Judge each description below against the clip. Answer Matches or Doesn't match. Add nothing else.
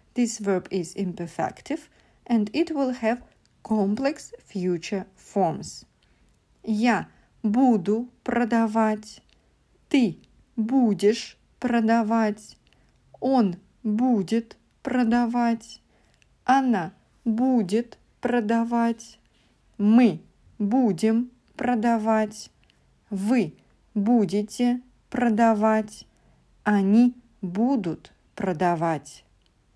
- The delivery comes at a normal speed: Doesn't match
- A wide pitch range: Doesn't match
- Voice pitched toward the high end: Matches